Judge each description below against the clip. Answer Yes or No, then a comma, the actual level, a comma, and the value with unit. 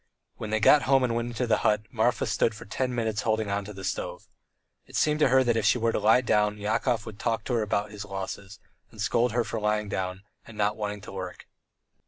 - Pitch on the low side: Yes, low, 110 Hz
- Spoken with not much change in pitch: Yes, narrow, 2.2 semitones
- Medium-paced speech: No, fast, 245 wpm